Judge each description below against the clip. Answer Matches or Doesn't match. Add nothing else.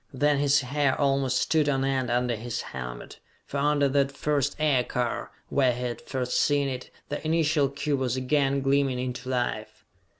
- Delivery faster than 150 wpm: Matches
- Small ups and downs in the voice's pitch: Matches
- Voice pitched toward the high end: Doesn't match